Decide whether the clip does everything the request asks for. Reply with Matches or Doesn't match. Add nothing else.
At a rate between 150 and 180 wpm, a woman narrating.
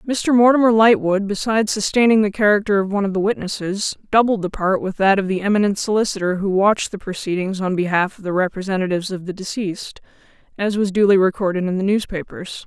Doesn't match